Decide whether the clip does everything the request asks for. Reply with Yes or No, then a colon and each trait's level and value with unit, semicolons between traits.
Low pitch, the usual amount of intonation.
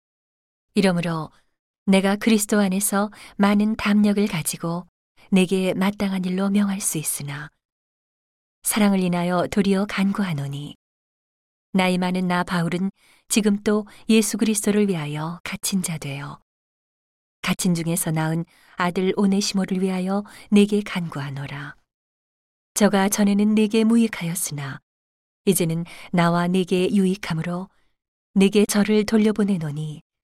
No: high, 190 Hz; average, 3.3 semitones